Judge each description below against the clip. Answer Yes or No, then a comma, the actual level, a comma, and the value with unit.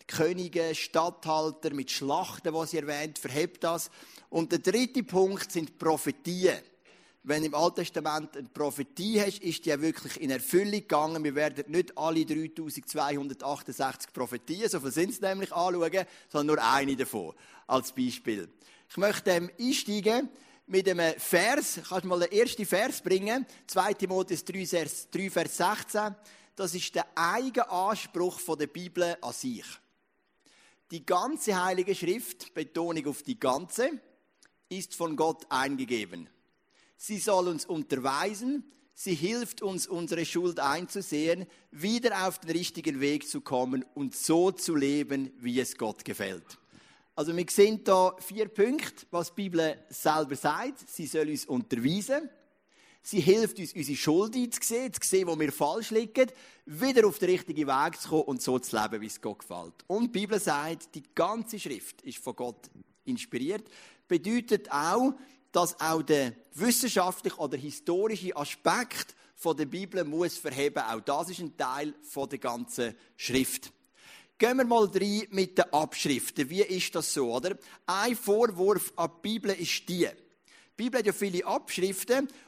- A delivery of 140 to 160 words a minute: Yes, average, 155 wpm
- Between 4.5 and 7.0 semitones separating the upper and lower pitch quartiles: Yes, wide, 5.4 semitones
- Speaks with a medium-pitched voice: Yes, medium, 175 Hz